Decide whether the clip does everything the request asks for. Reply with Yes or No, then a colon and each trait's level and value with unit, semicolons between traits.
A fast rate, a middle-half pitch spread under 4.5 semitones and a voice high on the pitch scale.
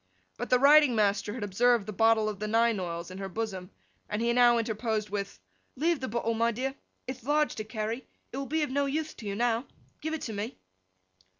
Yes: fast, 225 wpm; average, 3.6 semitones; high, 230 Hz